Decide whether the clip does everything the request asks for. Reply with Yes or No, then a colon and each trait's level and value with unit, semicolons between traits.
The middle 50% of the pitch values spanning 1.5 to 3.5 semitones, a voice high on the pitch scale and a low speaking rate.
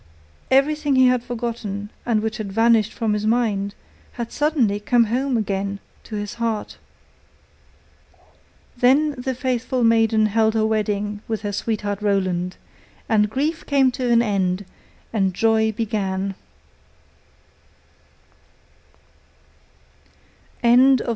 Yes: average, 3.0 semitones; high, 220 Hz; slow, 110 wpm